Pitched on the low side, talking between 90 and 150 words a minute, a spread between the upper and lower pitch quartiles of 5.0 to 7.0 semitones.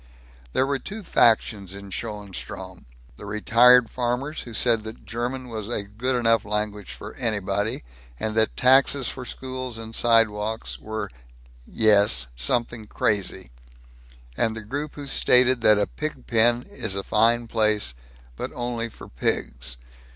No: low, 115 Hz; average, 145 wpm; average, 2.9 semitones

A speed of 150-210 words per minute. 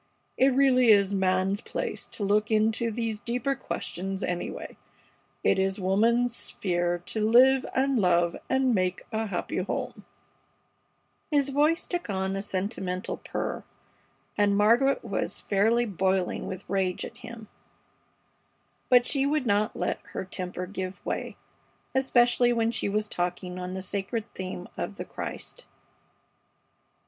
No: average, 140 wpm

